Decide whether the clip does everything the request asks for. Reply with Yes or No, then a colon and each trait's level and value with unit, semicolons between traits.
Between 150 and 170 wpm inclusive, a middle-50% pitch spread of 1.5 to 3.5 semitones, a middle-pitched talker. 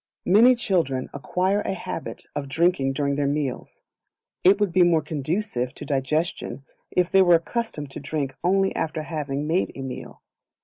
No: average, 165 wpm; average, 4.9 semitones; medium, 160 Hz